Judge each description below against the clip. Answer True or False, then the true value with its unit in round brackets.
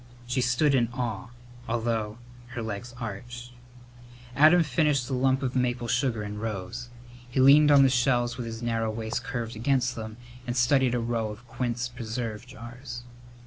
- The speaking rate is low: False (165 wpm)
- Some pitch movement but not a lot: False (2.0 semitones)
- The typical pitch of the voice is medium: False (120 Hz)